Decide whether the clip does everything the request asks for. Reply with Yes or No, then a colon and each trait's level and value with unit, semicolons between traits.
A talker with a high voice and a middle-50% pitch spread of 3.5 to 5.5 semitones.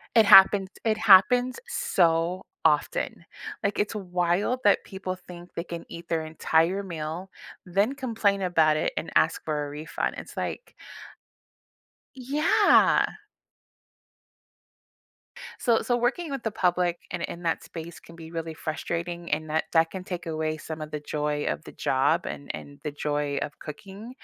No: medium, 175 Hz; average, 4.1 semitones